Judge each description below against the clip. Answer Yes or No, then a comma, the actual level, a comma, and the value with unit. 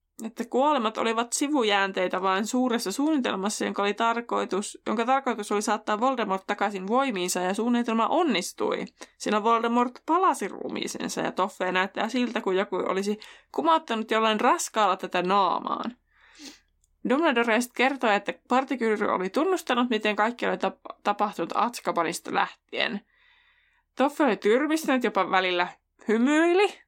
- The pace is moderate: Yes, average, 125 wpm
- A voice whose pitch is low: No, high, 230 Hz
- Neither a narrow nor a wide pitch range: Yes, average, 4.7 semitones